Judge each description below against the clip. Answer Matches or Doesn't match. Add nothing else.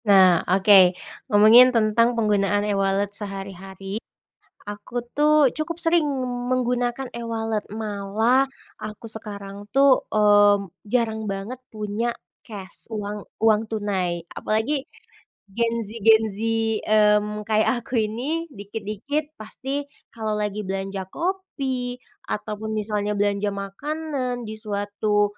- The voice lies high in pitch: Matches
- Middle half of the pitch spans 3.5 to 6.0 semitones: Doesn't match